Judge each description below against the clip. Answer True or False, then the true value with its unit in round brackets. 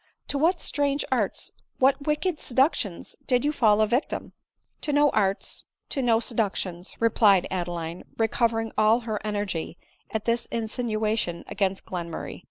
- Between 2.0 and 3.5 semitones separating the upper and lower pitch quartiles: False (4.7 semitones)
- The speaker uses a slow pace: False (170 wpm)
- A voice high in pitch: True (225 Hz)